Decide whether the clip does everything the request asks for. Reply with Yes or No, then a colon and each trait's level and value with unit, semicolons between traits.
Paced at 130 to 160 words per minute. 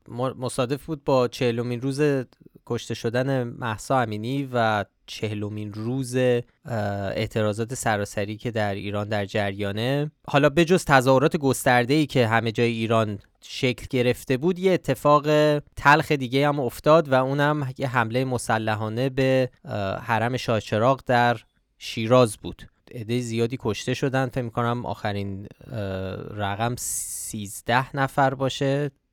No: average, 120 wpm